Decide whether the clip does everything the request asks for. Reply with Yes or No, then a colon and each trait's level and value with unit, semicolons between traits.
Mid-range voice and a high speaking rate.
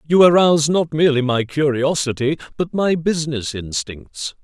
No: medium, 145 Hz; slow, 135 wpm